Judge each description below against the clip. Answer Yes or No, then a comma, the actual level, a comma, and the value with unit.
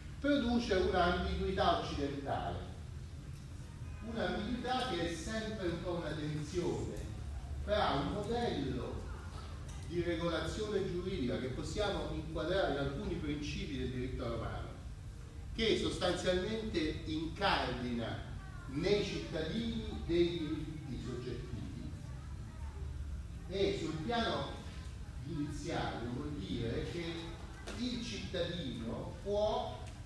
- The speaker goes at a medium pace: No, slow, 85 wpm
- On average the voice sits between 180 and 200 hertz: No, medium, 140 Hz